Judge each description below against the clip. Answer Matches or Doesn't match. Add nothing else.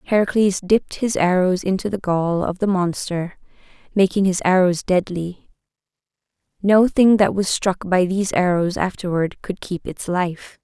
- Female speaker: Matches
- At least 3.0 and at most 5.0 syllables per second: Matches